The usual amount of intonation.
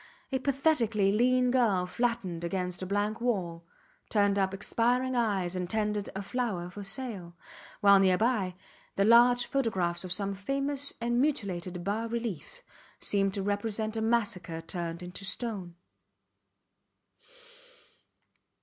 Yes: average, 4.5 semitones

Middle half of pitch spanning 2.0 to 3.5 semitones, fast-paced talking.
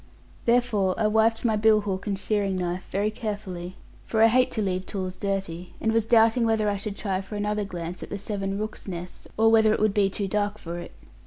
Yes: narrow, 2.5 semitones; fast, 225 wpm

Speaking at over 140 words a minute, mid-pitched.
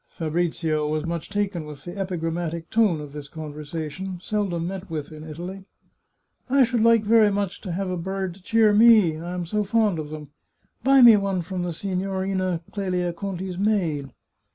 Yes: average, 180 wpm; medium, 180 Hz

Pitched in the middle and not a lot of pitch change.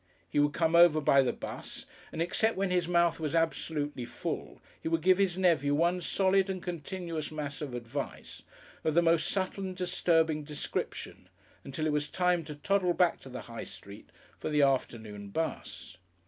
No: medium, 160 Hz; average, 3.6 semitones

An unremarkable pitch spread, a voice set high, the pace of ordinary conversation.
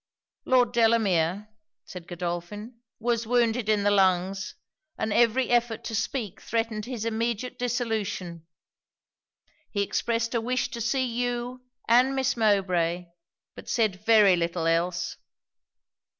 No: average, 4.1 semitones; high, 220 Hz; slow, 120 wpm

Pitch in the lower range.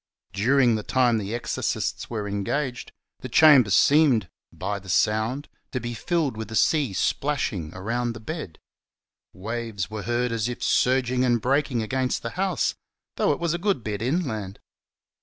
Yes: low, 120 Hz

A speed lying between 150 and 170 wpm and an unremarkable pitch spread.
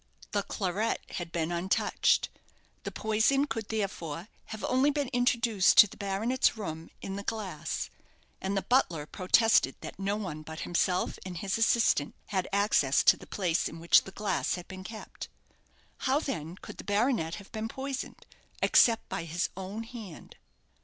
Yes: average, 165 wpm; average, 4.4 semitones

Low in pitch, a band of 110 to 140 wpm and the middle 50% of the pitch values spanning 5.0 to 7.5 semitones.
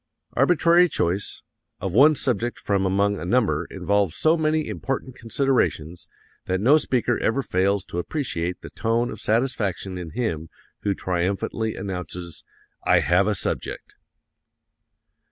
Yes: low, 105 Hz; slow, 135 wpm; wide, 5.6 semitones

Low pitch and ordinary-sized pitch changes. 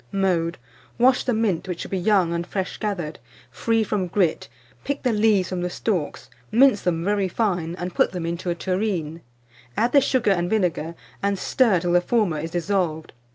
No: medium, 185 Hz; average, 3.8 semitones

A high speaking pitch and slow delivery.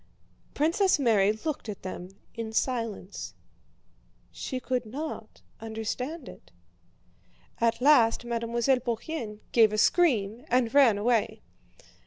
Yes: high, 235 Hz; slow, 110 wpm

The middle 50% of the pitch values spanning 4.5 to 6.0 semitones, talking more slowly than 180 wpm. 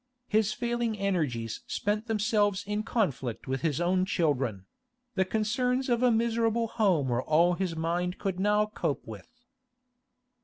Yes: average, 5.3 semitones; average, 145 wpm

